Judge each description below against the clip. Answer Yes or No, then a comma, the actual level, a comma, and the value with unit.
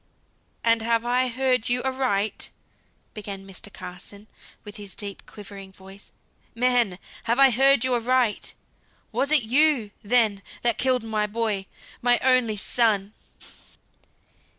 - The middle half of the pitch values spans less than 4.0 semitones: Yes, average, 3.6 semitones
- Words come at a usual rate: No, slow, 125 wpm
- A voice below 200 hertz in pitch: No, high, 230 Hz